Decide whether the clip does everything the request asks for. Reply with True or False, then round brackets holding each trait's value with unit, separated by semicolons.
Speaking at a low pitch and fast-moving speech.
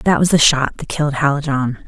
False (145 Hz; 225 wpm)